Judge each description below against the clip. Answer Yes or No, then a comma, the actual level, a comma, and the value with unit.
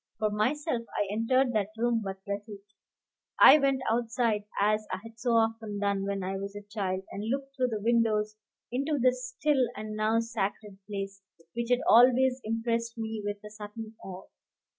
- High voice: Yes, high, 225 Hz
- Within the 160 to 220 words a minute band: Yes, average, 175 wpm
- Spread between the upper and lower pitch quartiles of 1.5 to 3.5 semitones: Yes, average, 2.9 semitones